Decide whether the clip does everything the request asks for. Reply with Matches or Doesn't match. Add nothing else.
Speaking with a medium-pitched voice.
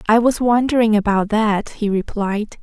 Doesn't match